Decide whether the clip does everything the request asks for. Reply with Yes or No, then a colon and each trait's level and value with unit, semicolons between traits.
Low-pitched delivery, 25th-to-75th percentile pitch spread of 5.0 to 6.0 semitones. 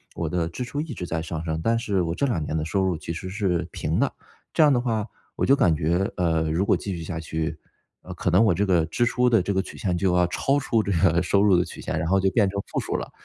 No: very low, 90 Hz; average, 3.9 semitones